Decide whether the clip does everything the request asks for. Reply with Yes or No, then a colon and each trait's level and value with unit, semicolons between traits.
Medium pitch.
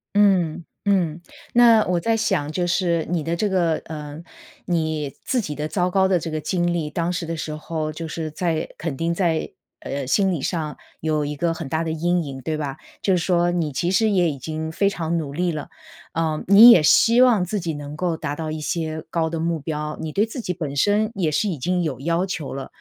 Yes: medium, 165 Hz